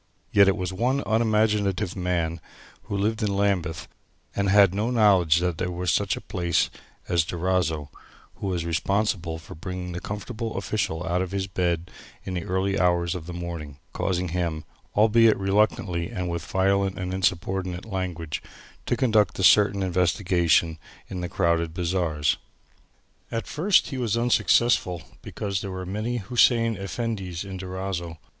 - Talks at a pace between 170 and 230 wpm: No, average, 150 wpm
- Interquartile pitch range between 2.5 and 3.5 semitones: Yes, average, 2.9 semitones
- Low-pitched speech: Yes, very low, 95 Hz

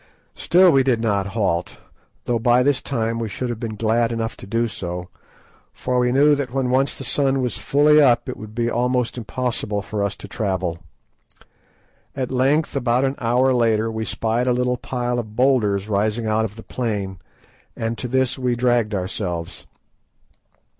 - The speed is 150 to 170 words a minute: No, average, 180 wpm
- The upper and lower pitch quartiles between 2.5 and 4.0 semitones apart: Yes, average, 2.9 semitones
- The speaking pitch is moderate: No, low, 120 Hz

